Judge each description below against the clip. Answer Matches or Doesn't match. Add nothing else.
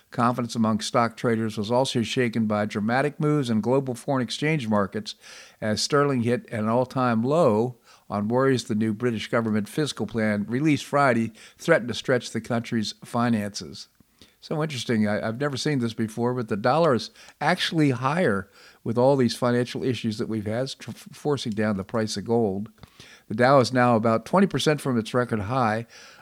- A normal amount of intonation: Matches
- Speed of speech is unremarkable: Matches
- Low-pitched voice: Matches